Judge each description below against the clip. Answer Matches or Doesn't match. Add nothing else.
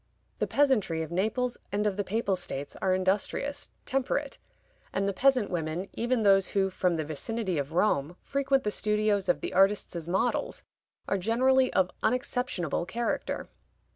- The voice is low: Doesn't match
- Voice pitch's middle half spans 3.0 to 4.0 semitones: Doesn't match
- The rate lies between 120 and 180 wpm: Matches